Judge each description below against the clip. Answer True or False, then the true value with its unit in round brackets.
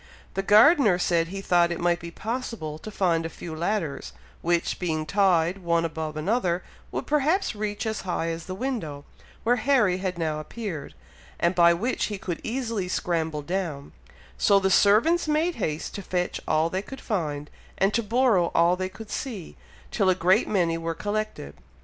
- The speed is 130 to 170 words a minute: False (180 wpm)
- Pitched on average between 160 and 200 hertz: True (185 Hz)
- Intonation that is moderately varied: True (4.4 semitones)